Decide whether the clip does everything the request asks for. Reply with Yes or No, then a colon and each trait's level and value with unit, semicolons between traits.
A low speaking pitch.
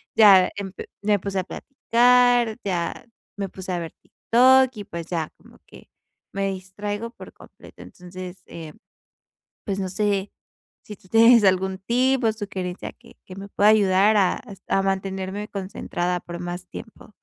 No: high, 195 Hz